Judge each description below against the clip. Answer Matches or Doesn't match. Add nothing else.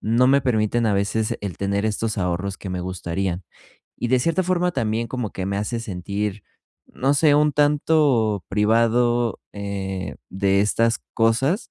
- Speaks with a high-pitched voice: Doesn't match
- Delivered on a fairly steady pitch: Doesn't match